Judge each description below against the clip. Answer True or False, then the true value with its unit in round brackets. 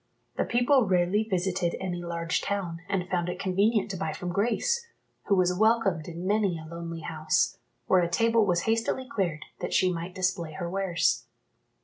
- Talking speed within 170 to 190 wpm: True (175 wpm)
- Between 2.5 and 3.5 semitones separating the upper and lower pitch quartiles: True (3.1 semitones)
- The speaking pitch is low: False (185 Hz)